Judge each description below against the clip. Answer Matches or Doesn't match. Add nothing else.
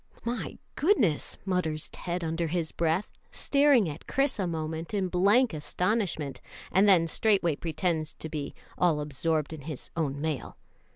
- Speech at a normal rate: Matches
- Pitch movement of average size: Matches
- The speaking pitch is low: Doesn't match